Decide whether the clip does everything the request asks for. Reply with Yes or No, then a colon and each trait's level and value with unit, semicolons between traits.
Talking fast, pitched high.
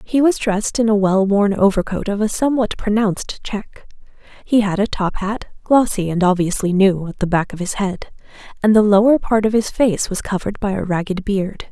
Yes: fast, 210 wpm; high, 205 Hz